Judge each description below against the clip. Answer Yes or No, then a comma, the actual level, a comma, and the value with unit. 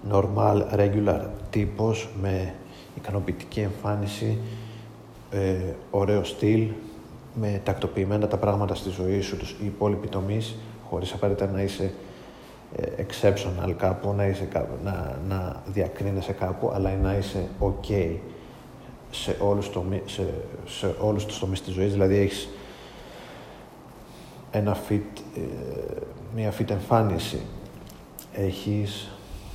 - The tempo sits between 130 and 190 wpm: No, slow, 115 wpm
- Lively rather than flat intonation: No, narrow, 1.5 semitones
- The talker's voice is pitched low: Yes, low, 100 Hz